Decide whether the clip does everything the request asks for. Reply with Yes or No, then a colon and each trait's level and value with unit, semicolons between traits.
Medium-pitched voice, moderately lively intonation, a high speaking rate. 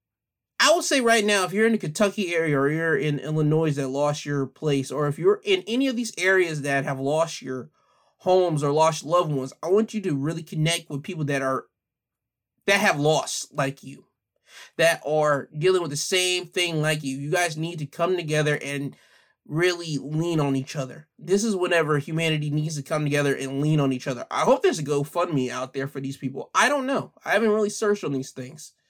Yes: medium, 155 Hz; average, 4.5 semitones; fast, 220 wpm